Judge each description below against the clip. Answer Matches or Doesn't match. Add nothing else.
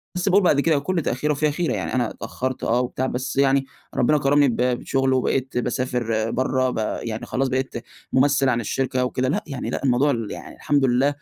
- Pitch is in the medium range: Doesn't match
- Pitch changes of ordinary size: Doesn't match